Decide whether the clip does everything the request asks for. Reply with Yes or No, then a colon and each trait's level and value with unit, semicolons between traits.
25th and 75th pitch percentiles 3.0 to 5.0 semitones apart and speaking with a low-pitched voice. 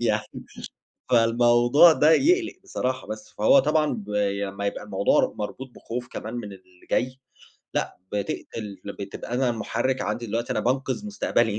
Yes: average, 4.0 semitones; low, 120 Hz